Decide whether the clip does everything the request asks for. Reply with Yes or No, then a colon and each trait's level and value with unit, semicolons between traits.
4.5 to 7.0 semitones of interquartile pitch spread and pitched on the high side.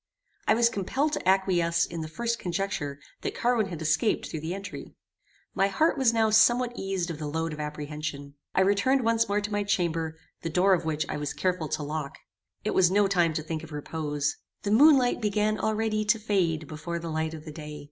No: average, 5.2 semitones; medium, 180 Hz